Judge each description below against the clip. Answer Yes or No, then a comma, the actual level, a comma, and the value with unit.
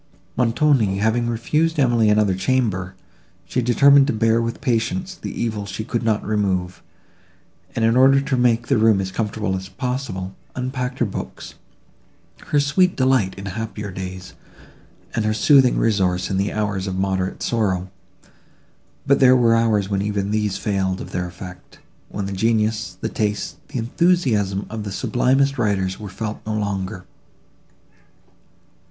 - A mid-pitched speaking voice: No, low, 110 Hz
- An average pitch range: Yes, average, 4.3 semitones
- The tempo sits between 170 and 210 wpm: No, average, 155 wpm